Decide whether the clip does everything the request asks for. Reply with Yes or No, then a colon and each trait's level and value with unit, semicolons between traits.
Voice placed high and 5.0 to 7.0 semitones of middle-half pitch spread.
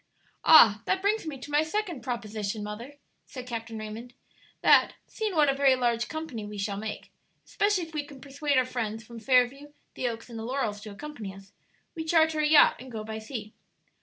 Yes: very high, 250 Hz; wide, 5.4 semitones